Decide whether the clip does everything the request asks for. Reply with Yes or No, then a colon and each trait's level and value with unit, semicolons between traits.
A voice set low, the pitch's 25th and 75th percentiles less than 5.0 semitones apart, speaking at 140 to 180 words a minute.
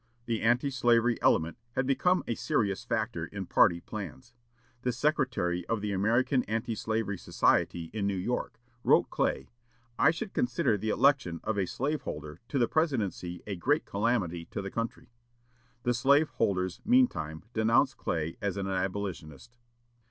No: low, 110 Hz; wide, 5.4 semitones; average, 155 wpm